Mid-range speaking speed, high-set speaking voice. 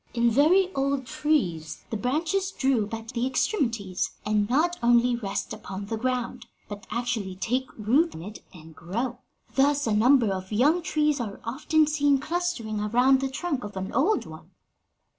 Yes: average, 165 wpm; high, 245 Hz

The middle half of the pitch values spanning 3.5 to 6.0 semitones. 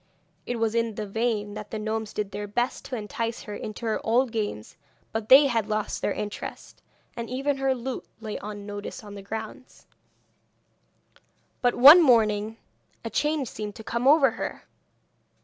No: average, 2.8 semitones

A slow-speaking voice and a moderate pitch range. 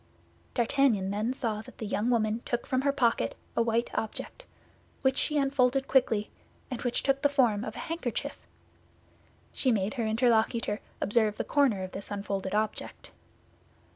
No: average, 160 wpm; average, 3.9 semitones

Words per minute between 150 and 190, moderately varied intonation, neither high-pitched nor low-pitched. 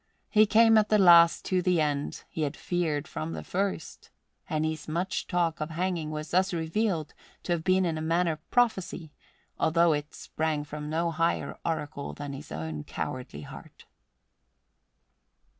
Yes: average, 160 wpm; average, 3.0 semitones; medium, 160 Hz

